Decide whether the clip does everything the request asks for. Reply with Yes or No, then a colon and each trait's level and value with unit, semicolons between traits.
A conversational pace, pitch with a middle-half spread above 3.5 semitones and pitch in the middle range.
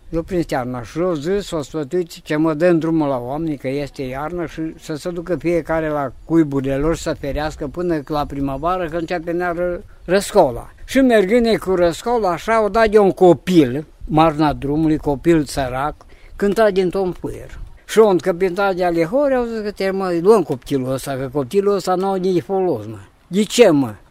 Yes: average, 195 wpm; average, 4.1 semitones; medium, 170 Hz